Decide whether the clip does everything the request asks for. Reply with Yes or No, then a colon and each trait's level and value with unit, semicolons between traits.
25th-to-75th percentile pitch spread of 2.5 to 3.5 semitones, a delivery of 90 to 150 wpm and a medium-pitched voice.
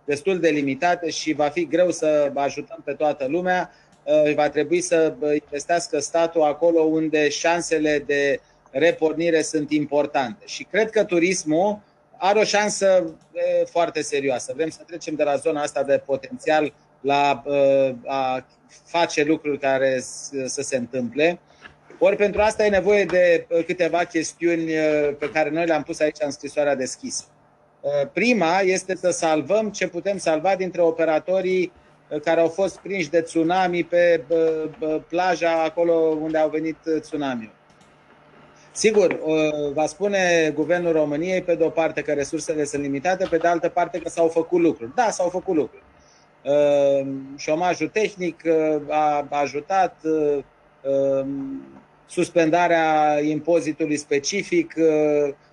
Yes: average, 2.8 semitones; average, 130 wpm; medium, 160 Hz